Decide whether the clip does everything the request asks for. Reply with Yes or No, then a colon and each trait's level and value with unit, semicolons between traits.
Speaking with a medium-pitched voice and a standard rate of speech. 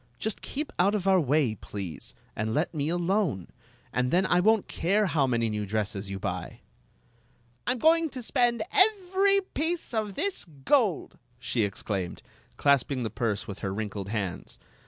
Yes: medium, 155 Hz; average, 165 wpm